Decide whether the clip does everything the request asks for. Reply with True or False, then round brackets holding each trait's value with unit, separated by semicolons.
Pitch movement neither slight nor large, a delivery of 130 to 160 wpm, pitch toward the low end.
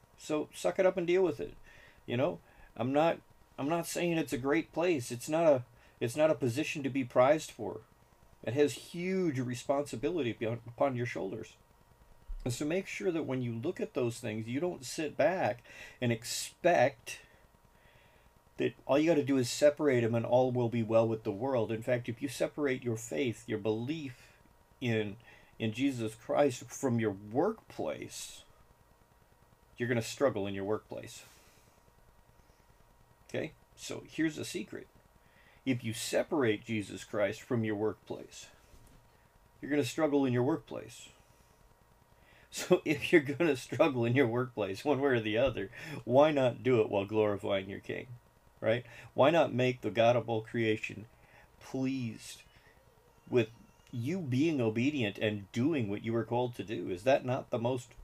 False (4.0 semitones; 170 wpm; 120 Hz)